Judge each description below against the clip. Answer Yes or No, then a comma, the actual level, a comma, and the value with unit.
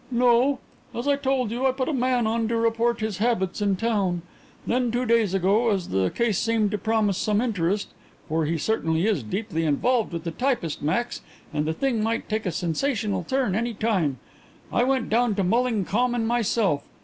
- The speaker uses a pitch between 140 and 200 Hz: No, high, 220 Hz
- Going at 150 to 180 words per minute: No, average, 195 wpm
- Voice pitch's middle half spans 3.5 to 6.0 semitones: Yes, average, 4.2 semitones